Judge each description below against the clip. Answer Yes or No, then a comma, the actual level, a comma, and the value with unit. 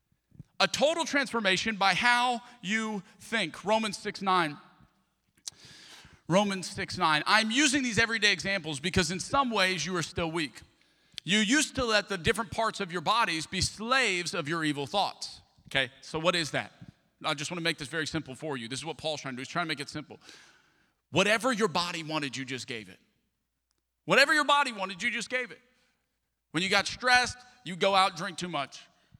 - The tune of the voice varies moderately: No, wide, 6.3 semitones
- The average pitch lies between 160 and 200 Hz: Yes, medium, 185 Hz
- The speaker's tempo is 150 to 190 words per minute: No, average, 200 wpm